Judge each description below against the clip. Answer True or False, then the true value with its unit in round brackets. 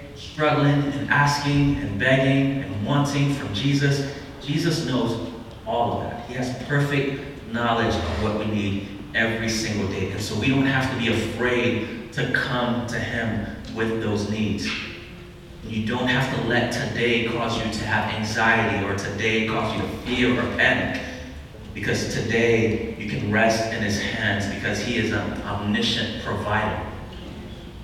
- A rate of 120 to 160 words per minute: True (155 wpm)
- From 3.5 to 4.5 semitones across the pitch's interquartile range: False (2.8 semitones)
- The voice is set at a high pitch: False (115 Hz)